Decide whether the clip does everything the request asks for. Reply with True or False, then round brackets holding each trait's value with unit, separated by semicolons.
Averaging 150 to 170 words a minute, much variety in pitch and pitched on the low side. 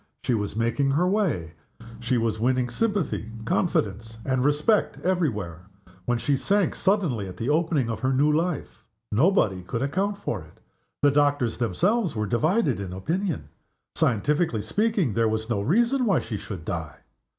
True (160 wpm; 8.2 semitones; 130 Hz)